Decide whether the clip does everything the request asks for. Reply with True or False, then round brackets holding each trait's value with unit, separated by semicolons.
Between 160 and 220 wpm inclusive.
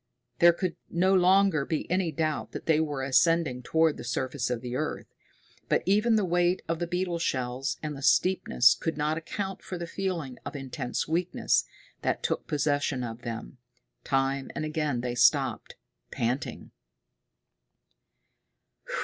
False (150 wpm)